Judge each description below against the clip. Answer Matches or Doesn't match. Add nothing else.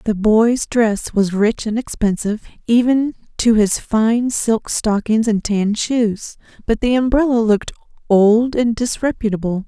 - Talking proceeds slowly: Doesn't match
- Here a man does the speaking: Doesn't match